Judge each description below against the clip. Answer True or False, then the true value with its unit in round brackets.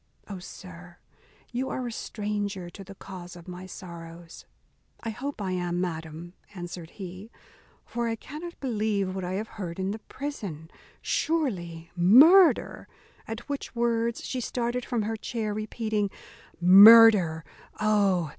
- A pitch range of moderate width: True (4.6 semitones)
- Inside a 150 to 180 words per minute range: False (140 wpm)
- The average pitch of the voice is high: True (200 Hz)